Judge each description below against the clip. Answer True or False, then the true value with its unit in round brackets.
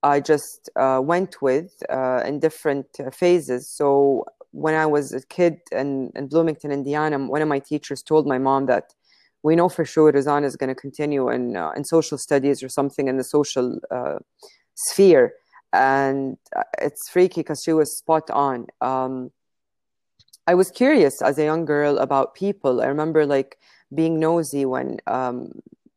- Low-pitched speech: False (145 Hz)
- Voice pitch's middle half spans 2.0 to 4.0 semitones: True (3.1 semitones)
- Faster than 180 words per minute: False (170 wpm)